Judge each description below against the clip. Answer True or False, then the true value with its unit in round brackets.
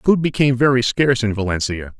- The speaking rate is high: False (180 wpm)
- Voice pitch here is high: False (120 Hz)